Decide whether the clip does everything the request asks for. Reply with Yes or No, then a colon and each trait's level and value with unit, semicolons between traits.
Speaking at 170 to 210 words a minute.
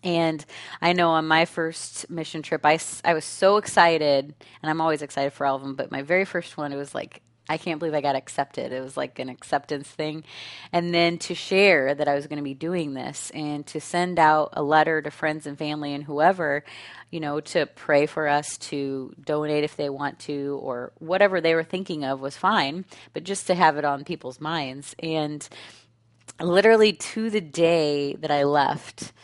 Yes: fast, 205 wpm